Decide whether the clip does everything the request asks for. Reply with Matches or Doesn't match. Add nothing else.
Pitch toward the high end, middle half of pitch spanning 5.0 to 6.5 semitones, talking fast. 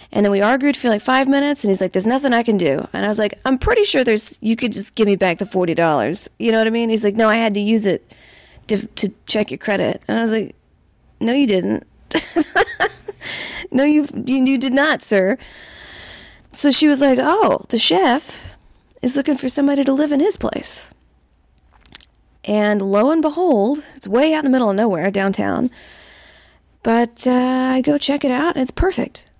Matches